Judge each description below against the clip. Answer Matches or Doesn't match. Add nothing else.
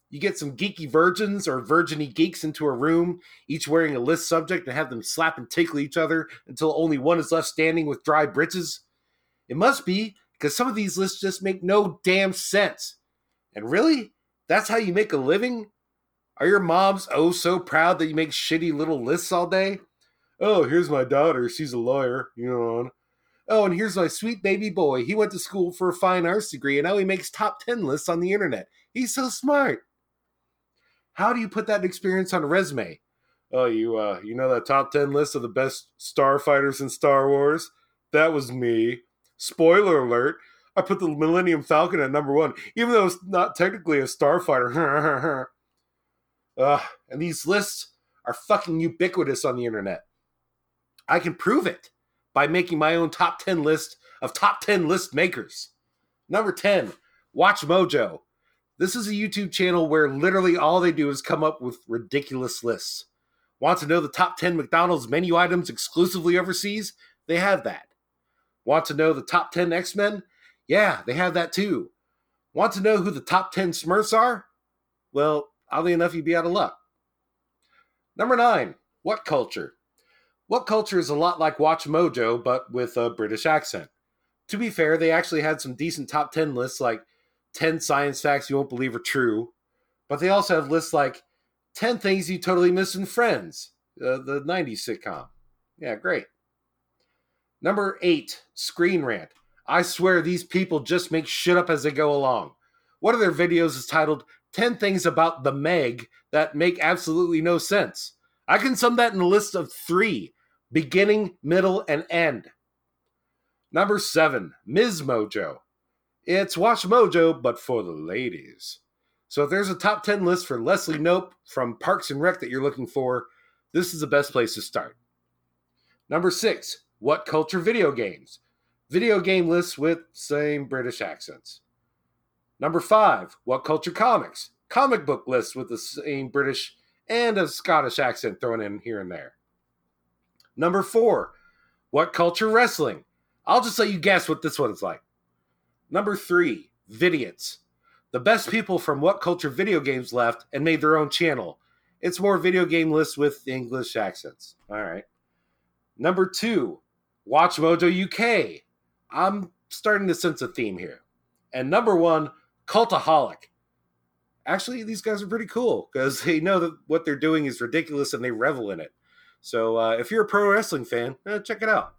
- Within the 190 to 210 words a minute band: Doesn't match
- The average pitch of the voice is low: Doesn't match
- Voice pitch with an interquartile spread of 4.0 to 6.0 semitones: Matches